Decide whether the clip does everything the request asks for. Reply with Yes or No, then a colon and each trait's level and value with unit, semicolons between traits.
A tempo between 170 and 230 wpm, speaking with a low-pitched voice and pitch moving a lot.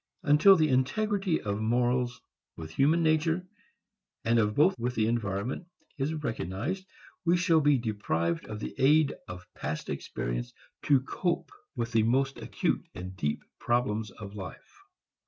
No: average, 145 wpm; low, 125 Hz; wide, 6.9 semitones